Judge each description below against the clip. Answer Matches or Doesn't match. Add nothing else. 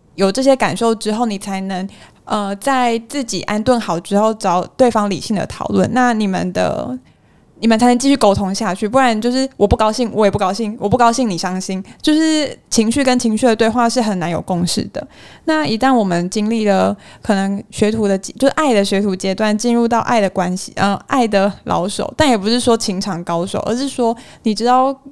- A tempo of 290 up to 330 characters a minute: Matches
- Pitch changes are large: Doesn't match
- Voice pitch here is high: Matches